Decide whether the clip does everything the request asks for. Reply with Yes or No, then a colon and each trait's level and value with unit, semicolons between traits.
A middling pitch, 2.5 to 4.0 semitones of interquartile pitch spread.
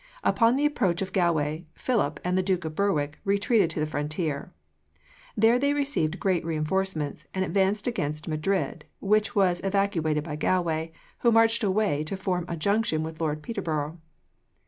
No: medium, 180 Hz; average, 4.6 semitones